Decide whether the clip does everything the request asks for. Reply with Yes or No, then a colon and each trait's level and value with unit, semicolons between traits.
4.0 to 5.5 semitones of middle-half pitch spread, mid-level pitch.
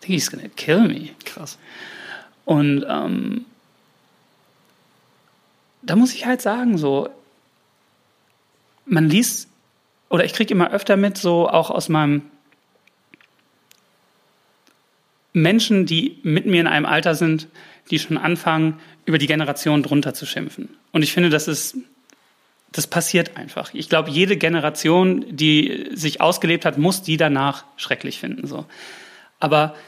Yes: average, 4.5 semitones; medium, 165 Hz